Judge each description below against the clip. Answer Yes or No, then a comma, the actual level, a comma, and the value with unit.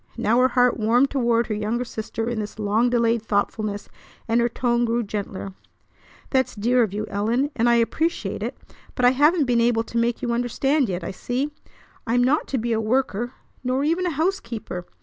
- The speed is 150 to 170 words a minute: No, average, 195 wpm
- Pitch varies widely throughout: No, narrow, 2.5 semitones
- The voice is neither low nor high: No, high, 235 Hz